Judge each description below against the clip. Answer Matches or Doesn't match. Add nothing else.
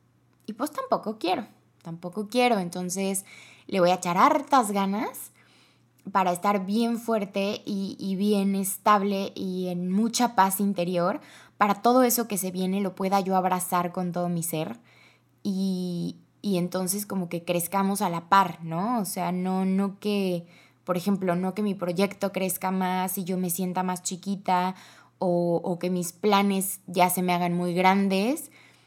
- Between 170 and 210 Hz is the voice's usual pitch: Matches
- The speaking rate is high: Doesn't match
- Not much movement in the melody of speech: Matches